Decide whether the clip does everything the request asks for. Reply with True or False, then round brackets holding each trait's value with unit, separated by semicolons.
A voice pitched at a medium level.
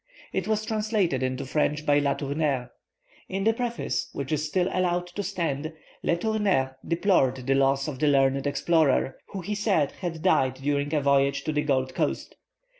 True (150 Hz)